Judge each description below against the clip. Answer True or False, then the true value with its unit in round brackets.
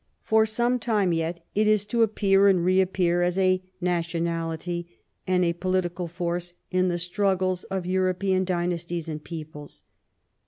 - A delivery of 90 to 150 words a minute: True (145 wpm)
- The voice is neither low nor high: True (180 Hz)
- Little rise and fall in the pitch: True (1.9 semitones)